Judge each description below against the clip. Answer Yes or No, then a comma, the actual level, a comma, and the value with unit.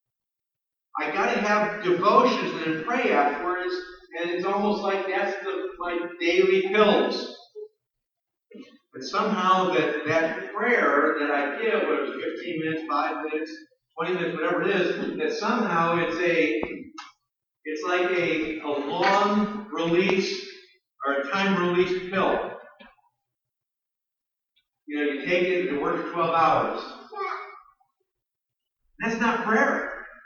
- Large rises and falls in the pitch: No, average, 4.5 semitones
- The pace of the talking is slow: Yes, slow, 125 wpm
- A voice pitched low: No, medium, 180 Hz